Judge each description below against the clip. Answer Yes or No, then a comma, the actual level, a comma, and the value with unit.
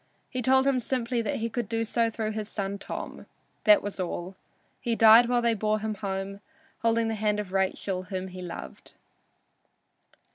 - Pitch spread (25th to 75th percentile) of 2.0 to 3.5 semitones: Yes, average, 2.9 semitones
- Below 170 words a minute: No, average, 180 wpm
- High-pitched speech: Yes, high, 215 Hz